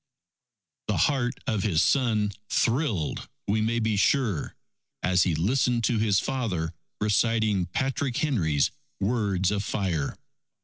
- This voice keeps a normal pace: No, slow, 125 wpm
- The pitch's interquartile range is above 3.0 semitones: Yes, average, 4.4 semitones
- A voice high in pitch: No, low, 105 Hz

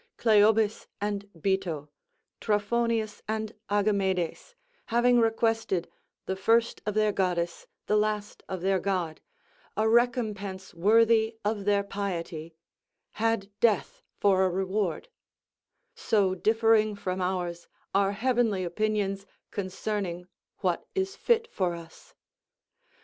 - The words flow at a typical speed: No, slow, 110 wpm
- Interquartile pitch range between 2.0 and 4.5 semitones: Yes, average, 2.8 semitones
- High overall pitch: Yes, high, 205 Hz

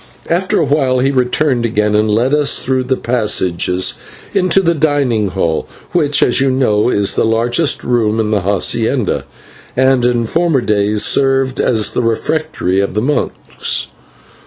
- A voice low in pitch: Yes, low, 125 Hz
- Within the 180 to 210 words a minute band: No, average, 160 wpm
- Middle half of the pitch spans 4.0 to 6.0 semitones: Yes, average, 4.5 semitones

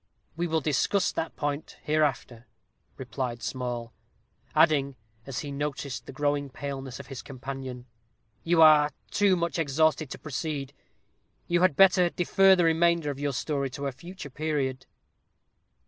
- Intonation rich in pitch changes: No, average, 3.3 semitones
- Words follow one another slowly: No, average, 145 wpm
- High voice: No, medium, 145 Hz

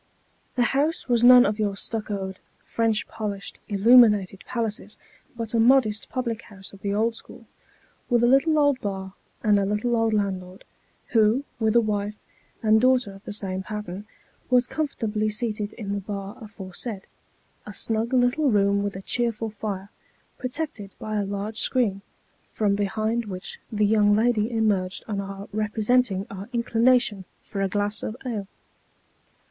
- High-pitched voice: Yes, high, 215 Hz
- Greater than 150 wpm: Yes, average, 160 wpm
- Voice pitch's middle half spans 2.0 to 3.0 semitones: Yes, average, 2.7 semitones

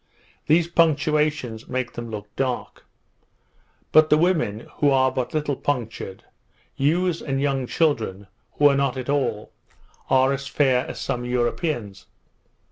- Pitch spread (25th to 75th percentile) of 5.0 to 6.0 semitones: No, average, 3.8 semitones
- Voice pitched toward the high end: No, low, 135 Hz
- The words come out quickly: No, slow, 135 wpm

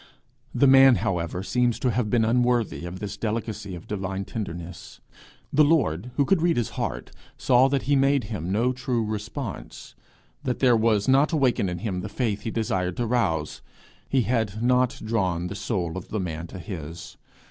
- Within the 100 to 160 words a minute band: No, average, 180 wpm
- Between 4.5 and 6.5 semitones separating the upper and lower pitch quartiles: Yes, average, 5.1 semitones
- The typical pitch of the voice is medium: No, low, 110 Hz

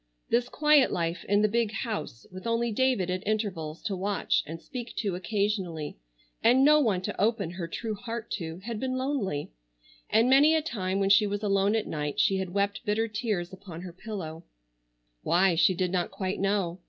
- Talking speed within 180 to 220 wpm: Yes, average, 190 wpm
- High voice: Yes, high, 200 Hz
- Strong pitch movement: No, average, 4.5 semitones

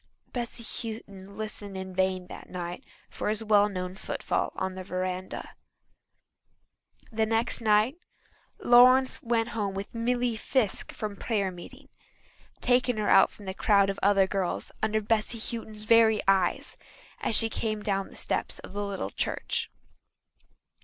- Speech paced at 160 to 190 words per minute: No, average, 145 wpm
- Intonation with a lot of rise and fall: No, average, 2.9 semitones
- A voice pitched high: Yes, high, 210 Hz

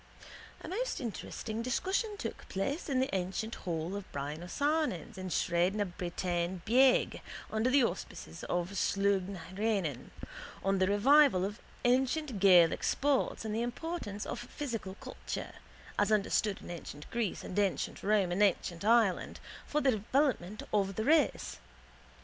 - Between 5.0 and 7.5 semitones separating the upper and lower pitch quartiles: Yes, wide, 5.4 semitones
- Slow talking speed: No, average, 150 wpm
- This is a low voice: No, high, 205 Hz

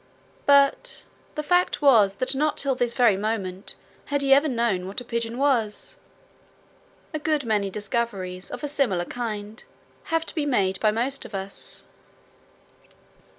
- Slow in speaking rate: No, average, 150 wpm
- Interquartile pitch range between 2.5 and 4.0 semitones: No, wide, 5.4 semitones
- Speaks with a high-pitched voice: Yes, high, 235 Hz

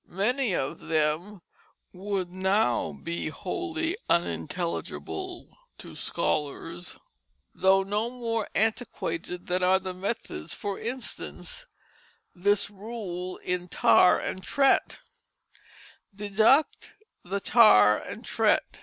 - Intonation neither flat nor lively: Yes, average, 4.2 semitones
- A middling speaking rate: No, slow, 100 wpm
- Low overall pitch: No, high, 190 Hz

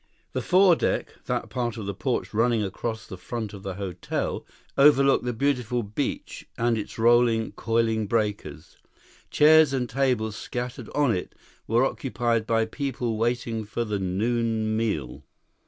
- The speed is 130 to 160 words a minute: Yes, average, 150 wpm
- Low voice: Yes, low, 115 Hz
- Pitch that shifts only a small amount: Yes, narrow, 2.3 semitones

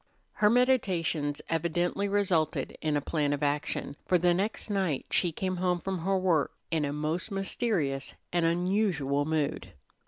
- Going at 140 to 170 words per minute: Yes, average, 155 wpm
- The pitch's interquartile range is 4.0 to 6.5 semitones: Yes, average, 4.4 semitones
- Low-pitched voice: No, medium, 170 Hz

